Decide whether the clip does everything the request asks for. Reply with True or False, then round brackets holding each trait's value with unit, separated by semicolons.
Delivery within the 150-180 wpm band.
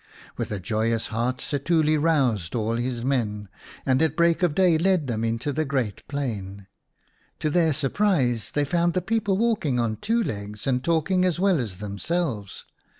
True (170 wpm)